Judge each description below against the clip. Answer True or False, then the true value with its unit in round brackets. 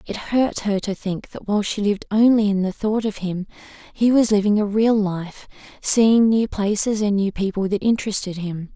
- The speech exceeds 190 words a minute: True (205 wpm)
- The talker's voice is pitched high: True (205 Hz)